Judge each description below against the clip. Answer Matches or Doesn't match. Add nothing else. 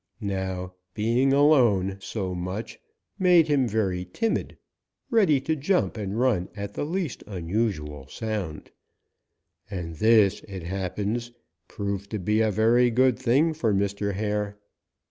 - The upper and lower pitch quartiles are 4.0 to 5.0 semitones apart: Matches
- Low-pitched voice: Matches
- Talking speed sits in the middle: Doesn't match